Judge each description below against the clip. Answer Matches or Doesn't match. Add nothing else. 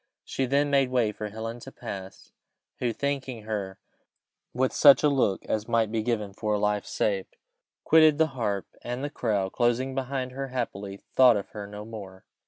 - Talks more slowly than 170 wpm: Doesn't match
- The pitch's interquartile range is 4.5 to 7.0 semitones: Doesn't match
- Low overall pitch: Matches